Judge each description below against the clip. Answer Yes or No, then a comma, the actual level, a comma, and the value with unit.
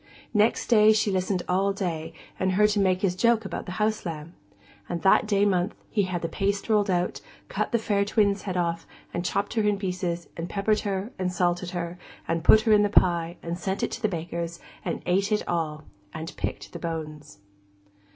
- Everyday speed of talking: No, fast, 210 wpm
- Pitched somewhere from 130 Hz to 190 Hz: Yes, medium, 185 Hz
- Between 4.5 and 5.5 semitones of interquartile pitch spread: No, average, 3.2 semitones